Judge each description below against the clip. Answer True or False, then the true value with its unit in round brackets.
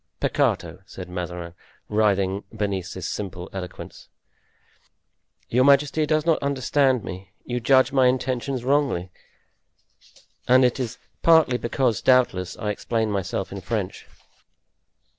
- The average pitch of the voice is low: True (120 Hz)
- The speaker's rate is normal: False (120 wpm)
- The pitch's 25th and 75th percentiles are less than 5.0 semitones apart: False (5.6 semitones)